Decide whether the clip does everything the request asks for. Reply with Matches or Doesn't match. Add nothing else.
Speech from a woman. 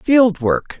Matches